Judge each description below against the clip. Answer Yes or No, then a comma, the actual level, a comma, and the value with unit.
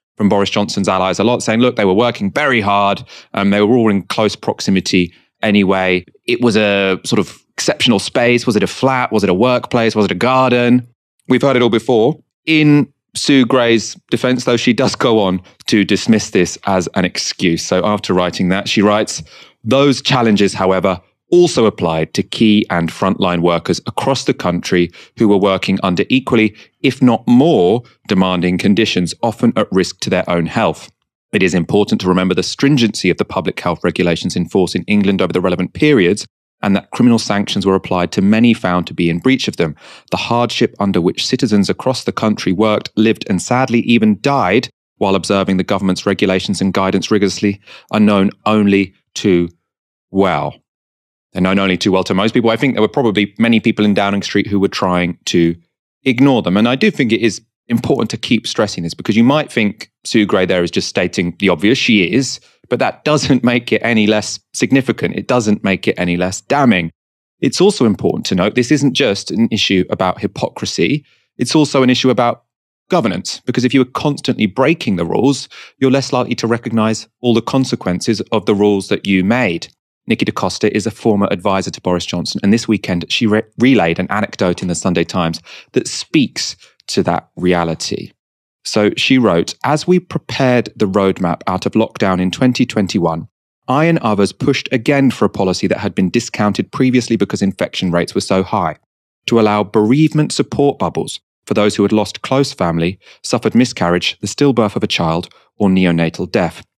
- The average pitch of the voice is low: Yes, low, 105 Hz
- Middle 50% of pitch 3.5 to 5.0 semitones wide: Yes, average, 4.7 semitones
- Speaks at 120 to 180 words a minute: No, average, 195 wpm